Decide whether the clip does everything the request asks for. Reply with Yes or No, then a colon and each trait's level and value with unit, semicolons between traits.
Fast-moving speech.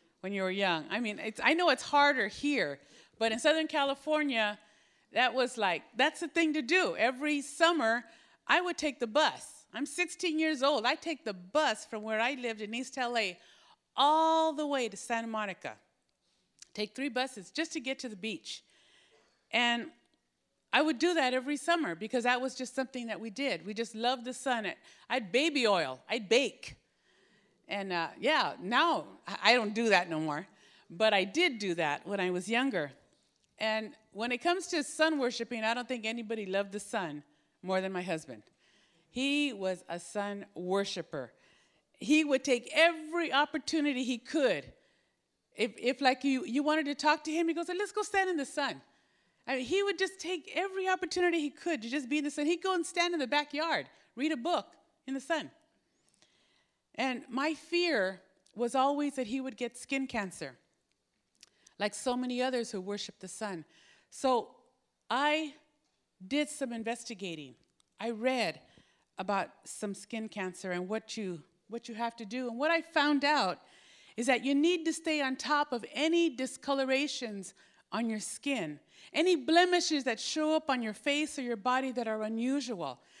No: average, 180 wpm